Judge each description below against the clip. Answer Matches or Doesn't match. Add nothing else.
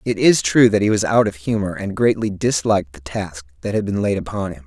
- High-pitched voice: Doesn't match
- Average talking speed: Doesn't match